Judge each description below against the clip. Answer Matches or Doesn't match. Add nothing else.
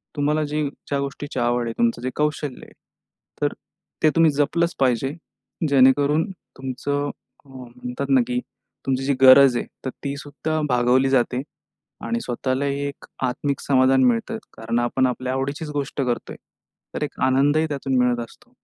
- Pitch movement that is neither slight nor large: Doesn't match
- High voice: Doesn't match